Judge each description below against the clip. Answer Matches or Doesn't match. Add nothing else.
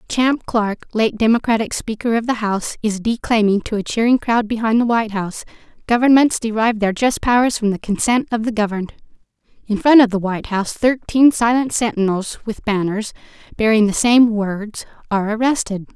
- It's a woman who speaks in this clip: Matches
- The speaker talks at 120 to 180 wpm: Matches